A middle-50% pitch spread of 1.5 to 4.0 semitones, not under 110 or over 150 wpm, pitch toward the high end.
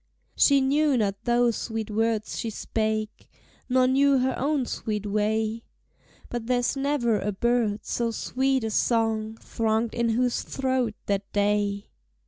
Yes: average, 2.8 semitones; average, 140 wpm; high, 230 Hz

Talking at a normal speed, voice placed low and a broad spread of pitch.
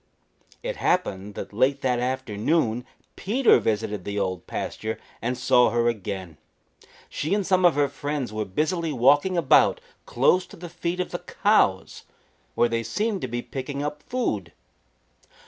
Yes: average, 155 wpm; low, 130 Hz; wide, 7.3 semitones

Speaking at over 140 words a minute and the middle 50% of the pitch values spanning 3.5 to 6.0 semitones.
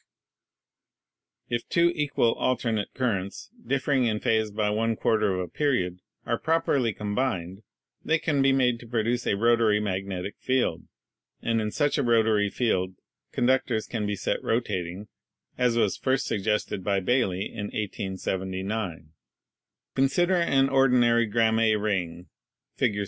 No: slow, 135 wpm; average, 4.0 semitones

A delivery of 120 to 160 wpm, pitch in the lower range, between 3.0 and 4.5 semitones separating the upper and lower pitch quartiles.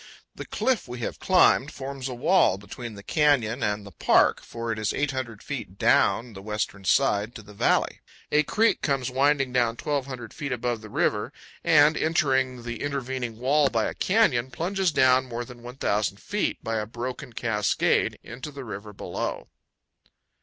No: average, 170 wpm; low, 125 Hz; average, 3.9 semitones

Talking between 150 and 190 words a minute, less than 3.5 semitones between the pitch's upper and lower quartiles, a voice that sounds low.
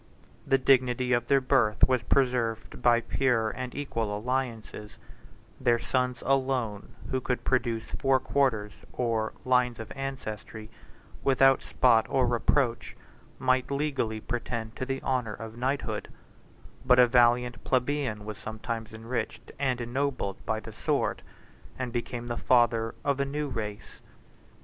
No: slow, 135 wpm; average, 2.7 semitones; low, 125 Hz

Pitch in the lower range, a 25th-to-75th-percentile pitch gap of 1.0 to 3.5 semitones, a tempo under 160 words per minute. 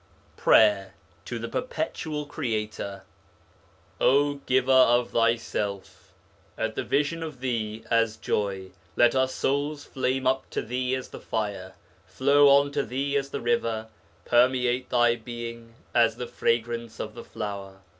Yes: low, 120 Hz; average, 3.2 semitones; average, 140 wpm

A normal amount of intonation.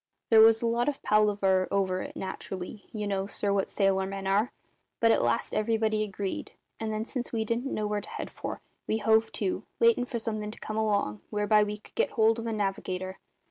No: narrow, 2.3 semitones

